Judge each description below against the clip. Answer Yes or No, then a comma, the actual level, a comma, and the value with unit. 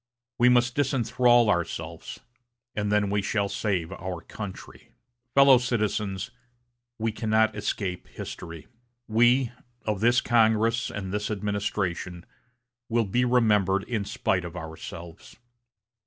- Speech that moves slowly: Yes, slow, 115 wpm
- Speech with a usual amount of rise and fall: Yes, average, 3.6 semitones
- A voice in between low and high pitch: No, low, 105 Hz